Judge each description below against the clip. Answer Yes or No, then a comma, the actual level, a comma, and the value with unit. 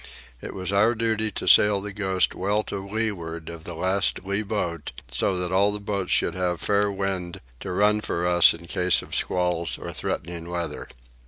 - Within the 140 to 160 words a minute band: No, average, 190 wpm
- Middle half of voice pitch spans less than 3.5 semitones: Yes, average, 2.8 semitones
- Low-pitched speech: Yes, very low, 95 Hz